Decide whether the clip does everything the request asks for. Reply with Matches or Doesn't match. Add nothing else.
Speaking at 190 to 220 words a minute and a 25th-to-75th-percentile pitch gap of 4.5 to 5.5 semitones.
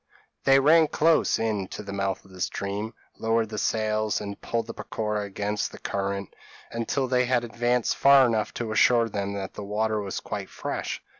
Doesn't match